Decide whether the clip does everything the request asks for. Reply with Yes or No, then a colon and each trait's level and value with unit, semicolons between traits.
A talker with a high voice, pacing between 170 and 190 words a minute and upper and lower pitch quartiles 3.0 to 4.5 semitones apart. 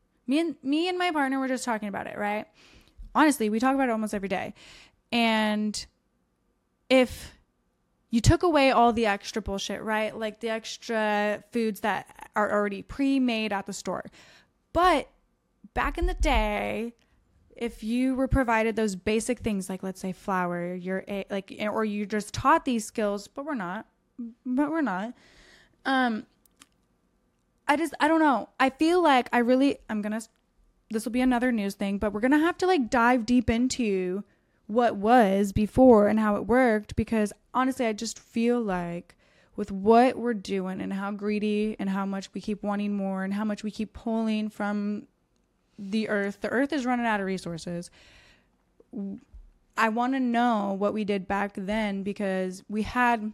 Yes: high, 220 Hz; average, 175 wpm; average, 3.5 semitones